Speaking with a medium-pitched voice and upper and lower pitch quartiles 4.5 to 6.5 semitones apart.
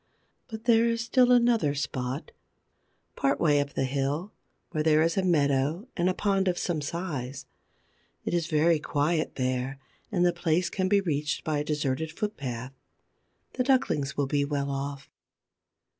Yes: medium, 155 Hz; average, 4.8 semitones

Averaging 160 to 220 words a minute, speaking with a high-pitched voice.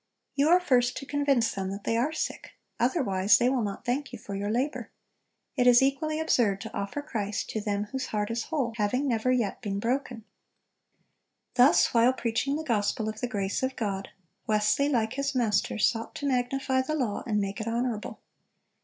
Yes: average, 190 wpm; high, 240 Hz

